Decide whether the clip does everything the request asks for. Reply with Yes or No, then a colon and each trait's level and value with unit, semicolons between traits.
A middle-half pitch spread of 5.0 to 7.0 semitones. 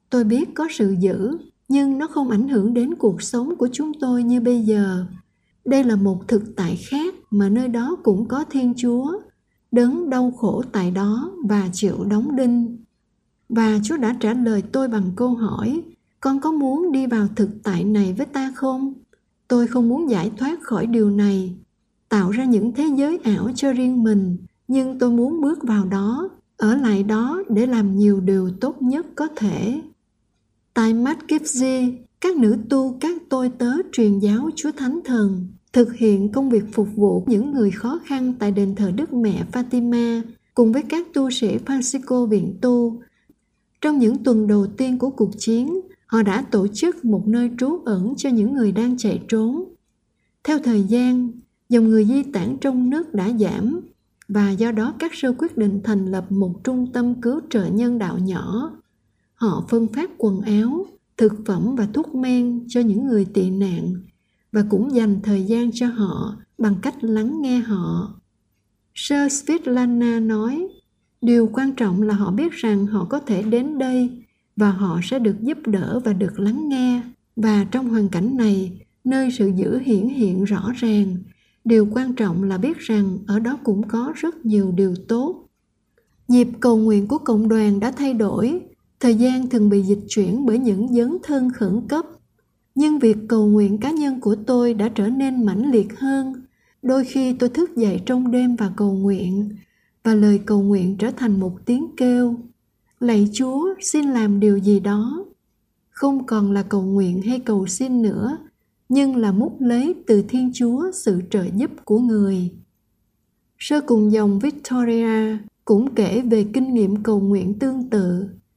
No: average, 4.0 semitones